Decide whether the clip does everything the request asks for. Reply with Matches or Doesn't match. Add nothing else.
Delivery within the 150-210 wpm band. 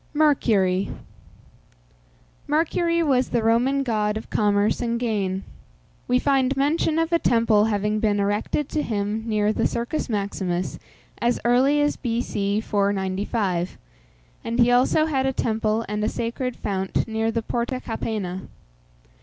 Doesn't match